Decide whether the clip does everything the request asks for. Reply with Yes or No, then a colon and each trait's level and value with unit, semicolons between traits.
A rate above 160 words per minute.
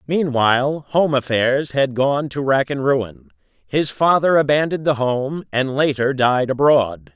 No: average, 150 wpm